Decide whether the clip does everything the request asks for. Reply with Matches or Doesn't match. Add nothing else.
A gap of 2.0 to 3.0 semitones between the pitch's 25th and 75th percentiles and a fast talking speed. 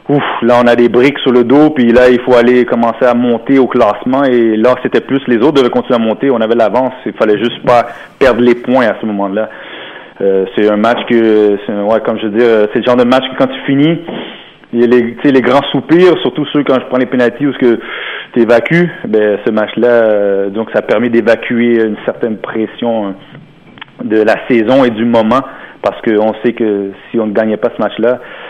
Matches